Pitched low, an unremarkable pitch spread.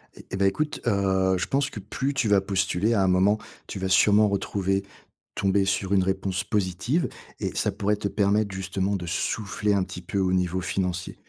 No: very low, 95 Hz; narrow, 1.6 semitones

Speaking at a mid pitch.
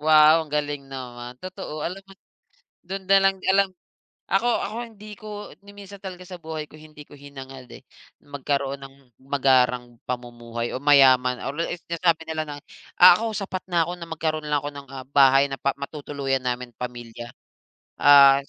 Yes: medium, 145 Hz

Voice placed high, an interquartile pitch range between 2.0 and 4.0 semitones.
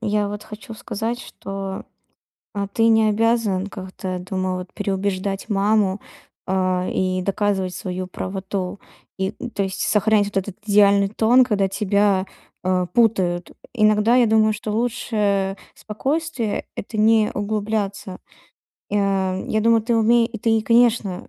Yes: high, 205 Hz; narrow, 2.4 semitones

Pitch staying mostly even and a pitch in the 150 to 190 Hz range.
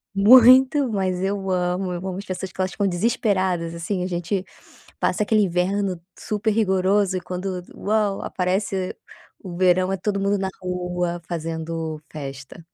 Yes: narrow, 2.2 semitones; medium, 185 Hz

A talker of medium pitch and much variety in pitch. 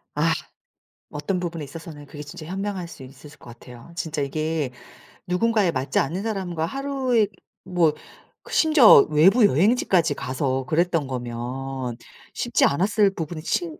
Yes: medium, 165 Hz; wide, 5.8 semitones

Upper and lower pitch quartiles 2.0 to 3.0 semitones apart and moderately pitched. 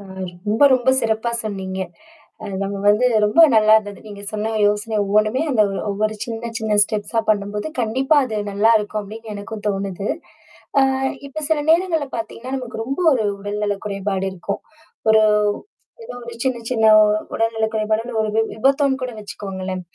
No: narrow, 2.5 semitones; high, 215 Hz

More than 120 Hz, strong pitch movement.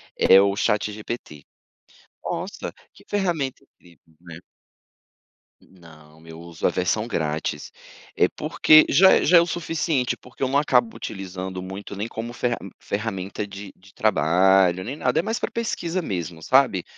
No: low, 100 Hz; wide, 7.2 semitones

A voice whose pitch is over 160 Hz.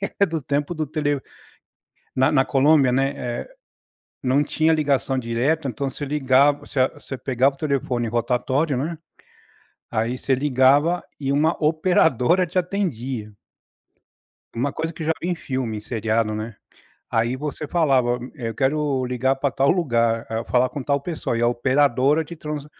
No: low, 135 Hz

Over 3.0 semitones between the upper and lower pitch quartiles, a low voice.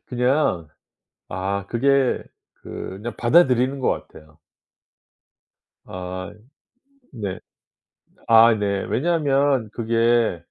Yes: average, 5.1 semitones; low, 115 Hz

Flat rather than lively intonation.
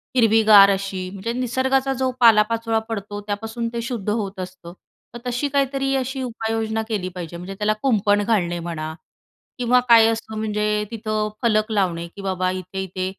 No: average, 3.4 semitones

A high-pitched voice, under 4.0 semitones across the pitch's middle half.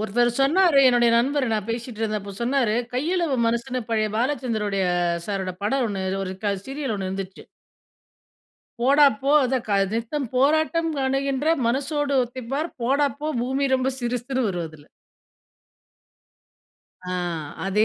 No: very high, 250 Hz; average, 4.4 semitones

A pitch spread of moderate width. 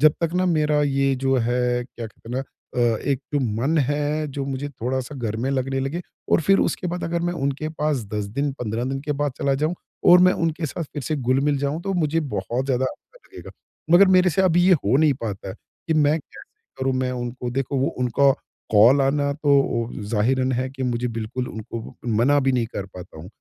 Yes: average, 3.5 semitones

